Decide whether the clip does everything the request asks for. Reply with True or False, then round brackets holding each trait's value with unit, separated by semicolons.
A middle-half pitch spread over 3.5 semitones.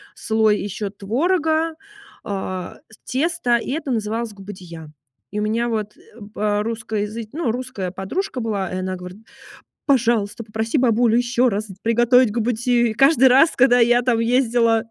False (3.0 semitones)